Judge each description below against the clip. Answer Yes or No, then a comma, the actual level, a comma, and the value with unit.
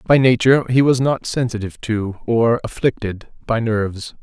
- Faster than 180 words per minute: No, average, 155 wpm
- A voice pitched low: Yes, low, 115 Hz